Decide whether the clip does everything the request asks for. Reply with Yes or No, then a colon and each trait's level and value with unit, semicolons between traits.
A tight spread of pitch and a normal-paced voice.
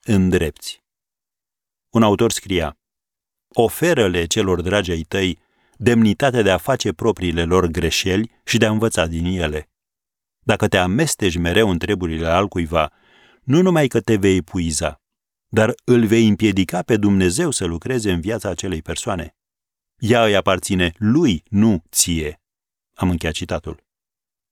No: average, 4.5 semitones; average, 140 wpm